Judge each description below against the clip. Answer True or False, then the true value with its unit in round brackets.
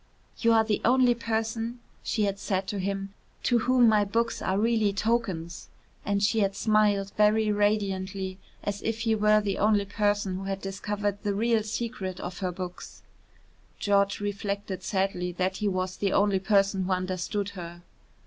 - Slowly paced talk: False (170 wpm)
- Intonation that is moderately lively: False (2.1 semitones)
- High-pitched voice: True (205 Hz)